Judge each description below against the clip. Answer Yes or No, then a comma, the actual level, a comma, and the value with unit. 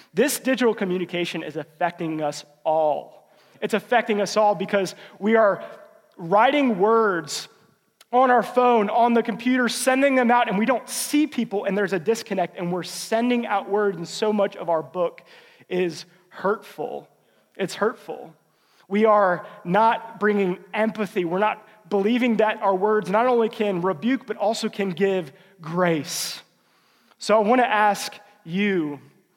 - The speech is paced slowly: No, average, 155 wpm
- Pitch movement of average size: Yes, average, 3.7 semitones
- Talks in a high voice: Yes, high, 205 Hz